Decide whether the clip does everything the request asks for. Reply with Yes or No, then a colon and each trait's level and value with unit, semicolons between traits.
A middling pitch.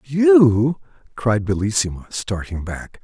No: low, 105 Hz